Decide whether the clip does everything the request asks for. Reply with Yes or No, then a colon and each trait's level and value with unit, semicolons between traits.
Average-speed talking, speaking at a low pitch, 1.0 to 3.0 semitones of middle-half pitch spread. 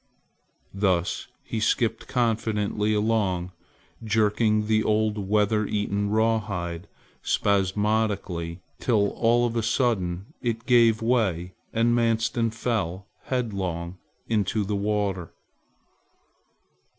No: slow, 95 wpm; low, 105 Hz; narrow, 2.6 semitones